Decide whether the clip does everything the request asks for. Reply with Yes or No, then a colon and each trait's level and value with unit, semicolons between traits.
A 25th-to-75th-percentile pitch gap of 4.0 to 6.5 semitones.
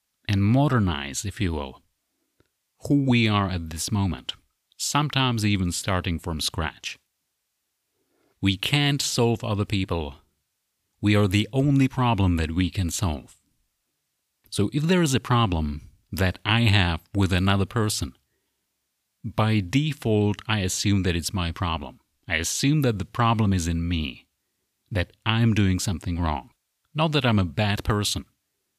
Yes: average, 4.5 semitones